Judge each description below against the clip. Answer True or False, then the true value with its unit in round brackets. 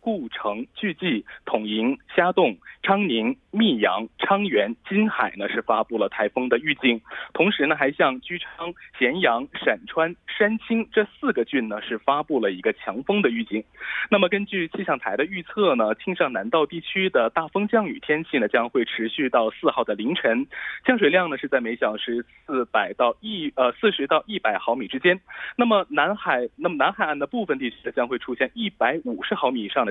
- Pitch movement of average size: False (7.5 semitones)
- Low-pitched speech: False (190 Hz)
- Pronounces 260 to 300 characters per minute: True (285 characters per minute)